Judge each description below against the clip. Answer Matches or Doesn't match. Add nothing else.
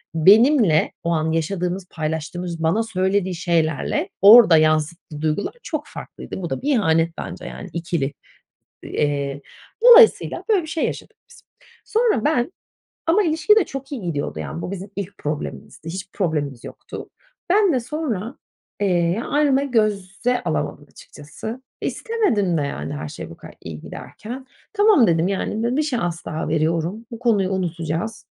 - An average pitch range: Doesn't match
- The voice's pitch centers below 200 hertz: Matches